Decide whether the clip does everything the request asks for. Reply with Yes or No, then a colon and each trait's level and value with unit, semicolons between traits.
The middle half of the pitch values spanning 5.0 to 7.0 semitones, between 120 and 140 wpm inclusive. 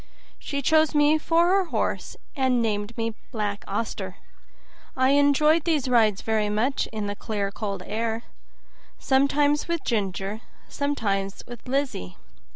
Yes: wide, 5.5 semitones; slow, 135 wpm